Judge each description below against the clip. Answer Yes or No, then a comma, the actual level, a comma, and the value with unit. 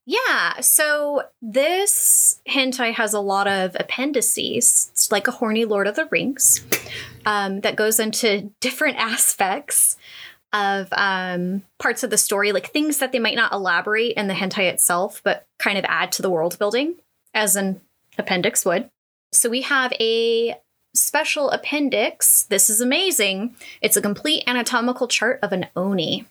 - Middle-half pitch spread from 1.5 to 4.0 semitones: No, wide, 5.6 semitones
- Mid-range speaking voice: No, high, 225 Hz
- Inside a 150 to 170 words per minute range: Yes, average, 155 wpm